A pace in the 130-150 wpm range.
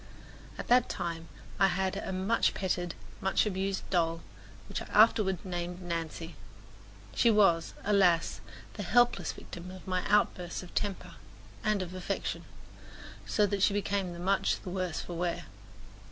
Yes: average, 145 wpm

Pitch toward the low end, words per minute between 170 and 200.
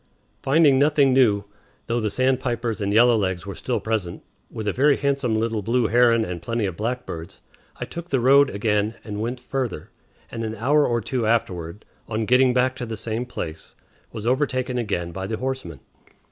Yes: low, 115 Hz; average, 180 wpm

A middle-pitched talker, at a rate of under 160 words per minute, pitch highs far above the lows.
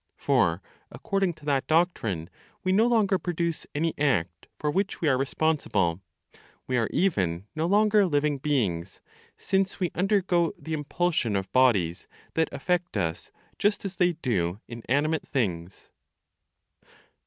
Yes: medium, 150 Hz; slow, 135 wpm; wide, 8.9 semitones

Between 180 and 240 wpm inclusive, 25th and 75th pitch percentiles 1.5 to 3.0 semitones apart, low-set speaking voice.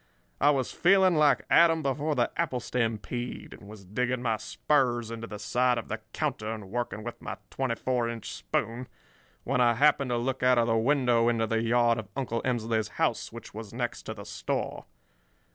Yes: average, 195 wpm; narrow, 2.6 semitones; low, 120 Hz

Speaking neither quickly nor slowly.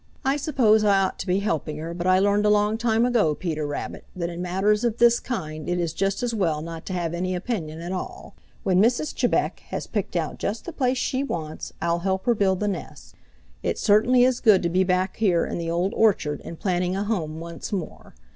No: fast, 230 wpm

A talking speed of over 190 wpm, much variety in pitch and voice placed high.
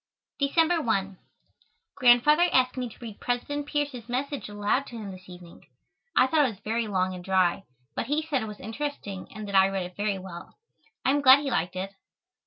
Yes: average, 200 wpm; wide, 6.4 semitones; high, 225 Hz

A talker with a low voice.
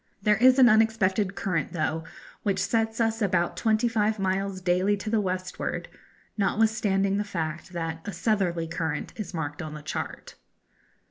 No: high, 195 Hz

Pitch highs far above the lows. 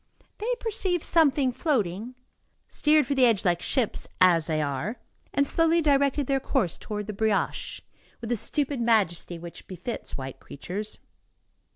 Yes: wide, 7.5 semitones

